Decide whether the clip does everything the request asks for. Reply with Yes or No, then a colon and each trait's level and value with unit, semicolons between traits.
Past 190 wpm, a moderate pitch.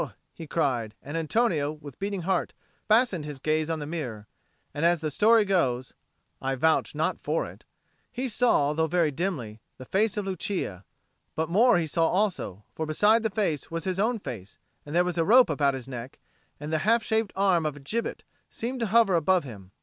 Yes: average, 200 wpm; medium, 165 Hz